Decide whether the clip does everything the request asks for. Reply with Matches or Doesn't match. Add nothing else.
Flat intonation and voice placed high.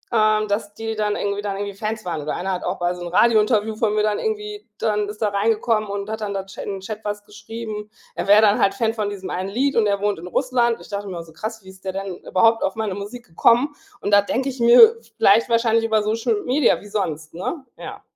Matches